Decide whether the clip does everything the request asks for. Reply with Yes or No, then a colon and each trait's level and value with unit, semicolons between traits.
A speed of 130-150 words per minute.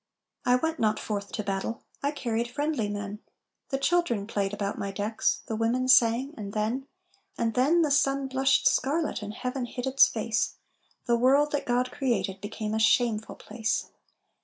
No: average, 170 wpm